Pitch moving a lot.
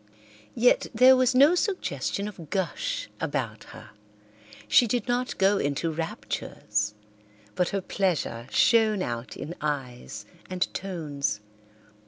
Yes: wide, 8.3 semitones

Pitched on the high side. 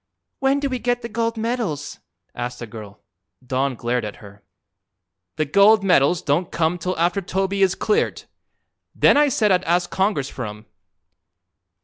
No: medium, 180 Hz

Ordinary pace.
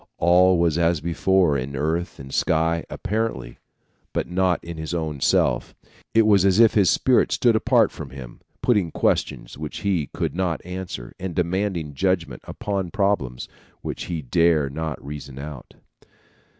Yes: average, 155 wpm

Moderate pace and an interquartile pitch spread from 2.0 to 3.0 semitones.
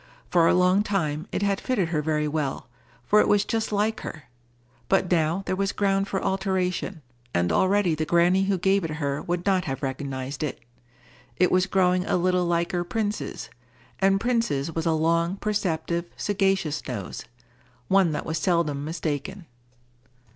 No: average, 160 wpm; average, 4.0 semitones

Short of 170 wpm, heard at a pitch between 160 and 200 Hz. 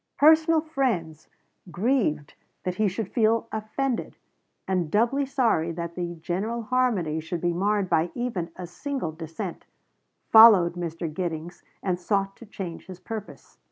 Yes: average, 140 wpm; high, 190 Hz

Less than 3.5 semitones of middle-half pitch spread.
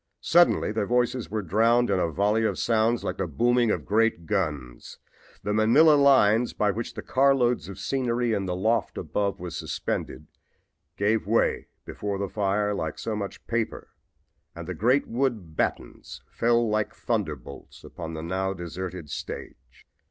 No: average, 4.1 semitones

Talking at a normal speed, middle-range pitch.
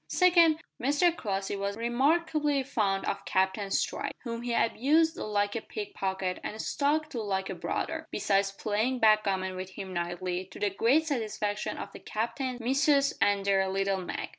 No: average, 165 wpm; high, 215 Hz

